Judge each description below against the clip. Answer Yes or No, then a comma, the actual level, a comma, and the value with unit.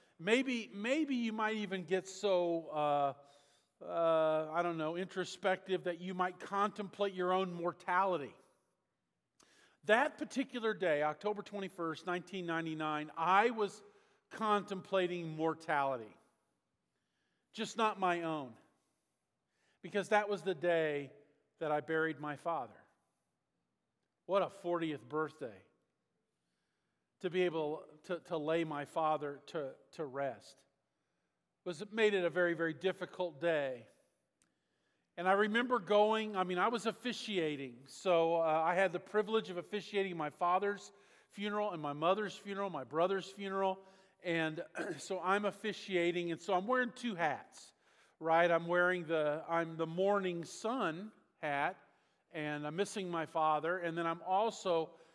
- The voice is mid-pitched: Yes, medium, 180 Hz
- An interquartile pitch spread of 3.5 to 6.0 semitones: Yes, average, 3.8 semitones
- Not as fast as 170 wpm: Yes, slow, 135 wpm